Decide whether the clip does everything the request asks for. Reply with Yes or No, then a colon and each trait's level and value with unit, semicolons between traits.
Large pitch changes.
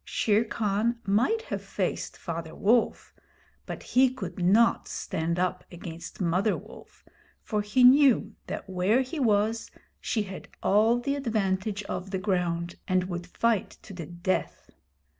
No: average, 4.3 semitones